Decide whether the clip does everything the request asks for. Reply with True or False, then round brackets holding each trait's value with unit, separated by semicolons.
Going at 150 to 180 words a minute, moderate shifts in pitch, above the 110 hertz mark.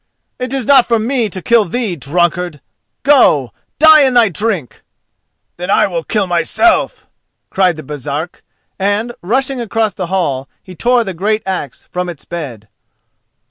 False (155 wpm; 5.7 semitones; 190 Hz)